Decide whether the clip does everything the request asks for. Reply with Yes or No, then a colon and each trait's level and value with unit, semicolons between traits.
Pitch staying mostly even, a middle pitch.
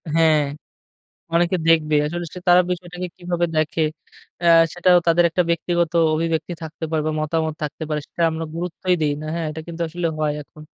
Yes: narrow, 1.9 semitones; medium, 165 Hz